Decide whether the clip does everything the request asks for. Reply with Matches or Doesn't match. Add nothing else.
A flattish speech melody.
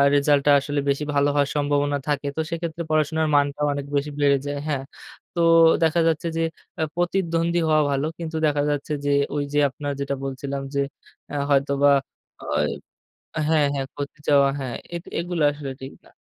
Matches